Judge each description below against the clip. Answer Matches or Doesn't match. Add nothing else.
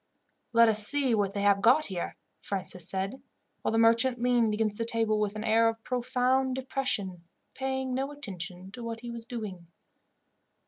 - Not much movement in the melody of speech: Doesn't match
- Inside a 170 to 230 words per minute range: Matches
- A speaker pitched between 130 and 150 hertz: Doesn't match